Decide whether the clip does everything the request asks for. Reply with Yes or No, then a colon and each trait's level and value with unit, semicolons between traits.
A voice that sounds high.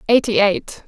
Yes: high, 210 Hz